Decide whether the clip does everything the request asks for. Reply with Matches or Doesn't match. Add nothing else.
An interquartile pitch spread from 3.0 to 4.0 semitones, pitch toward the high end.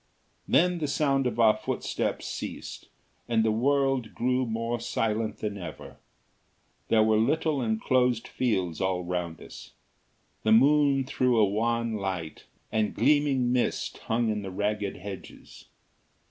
Doesn't match